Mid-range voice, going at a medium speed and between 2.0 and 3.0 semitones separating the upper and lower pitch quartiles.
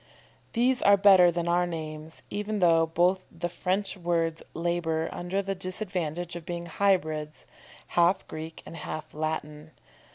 Yes: medium, 175 Hz; average, 150 wpm; narrow, 2.6 semitones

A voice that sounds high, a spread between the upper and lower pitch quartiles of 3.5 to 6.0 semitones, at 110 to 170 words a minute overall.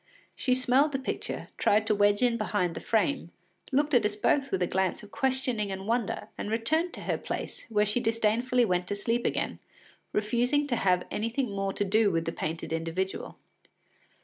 No: high, 215 Hz; average, 4.2 semitones; average, 190 wpm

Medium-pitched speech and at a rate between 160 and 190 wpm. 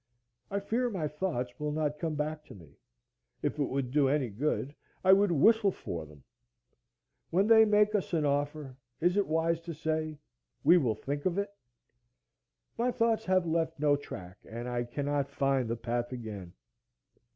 Yes: medium, 150 Hz; average, 175 wpm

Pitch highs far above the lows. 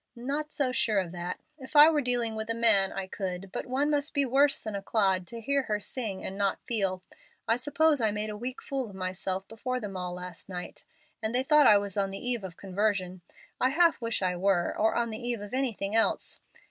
No: average, 4.8 semitones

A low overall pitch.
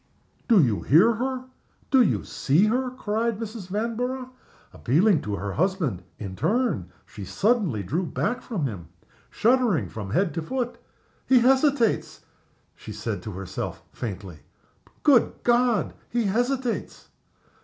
No: high, 210 Hz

